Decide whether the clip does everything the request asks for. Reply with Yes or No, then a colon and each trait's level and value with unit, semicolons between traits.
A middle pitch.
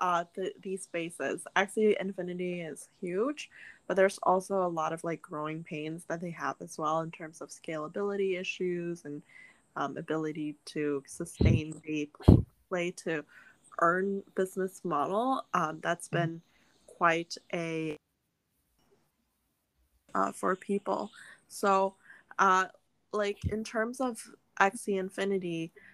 Yes: medium, 175 Hz